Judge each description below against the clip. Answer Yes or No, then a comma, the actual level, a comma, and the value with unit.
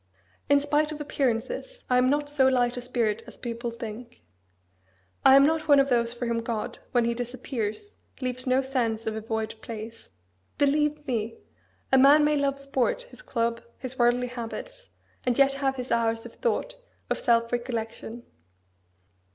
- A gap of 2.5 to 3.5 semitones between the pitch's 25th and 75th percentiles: Yes, average, 3.2 semitones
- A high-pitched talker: Yes, very high, 250 Hz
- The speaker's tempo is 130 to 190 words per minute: Yes, average, 170 wpm